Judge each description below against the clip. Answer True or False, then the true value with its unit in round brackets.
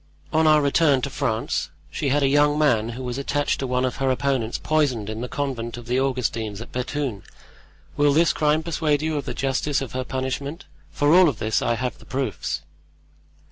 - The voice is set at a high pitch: False (135 Hz)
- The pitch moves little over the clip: False (3.4 semitones)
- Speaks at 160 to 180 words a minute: False (200 wpm)